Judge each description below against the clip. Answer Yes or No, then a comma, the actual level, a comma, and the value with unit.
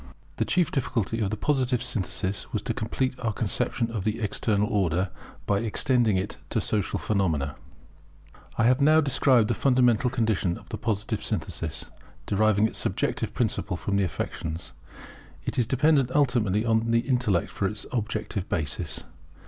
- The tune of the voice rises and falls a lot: No, average, 3.8 semitones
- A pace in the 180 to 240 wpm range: No, average, 155 wpm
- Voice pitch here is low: Yes, low, 110 Hz